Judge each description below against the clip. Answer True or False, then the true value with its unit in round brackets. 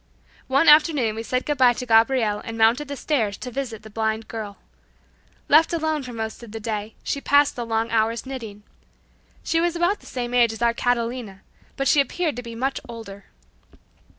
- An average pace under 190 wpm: False (195 wpm)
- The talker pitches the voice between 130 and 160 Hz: False (235 Hz)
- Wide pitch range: False (3.7 semitones)